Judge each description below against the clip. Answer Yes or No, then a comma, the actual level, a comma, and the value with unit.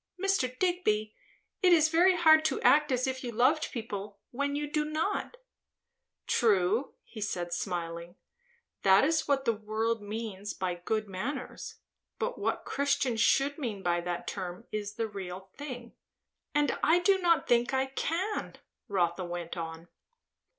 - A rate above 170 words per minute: No, average, 150 wpm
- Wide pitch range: Yes, wide, 7.3 semitones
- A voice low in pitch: No, high, 235 Hz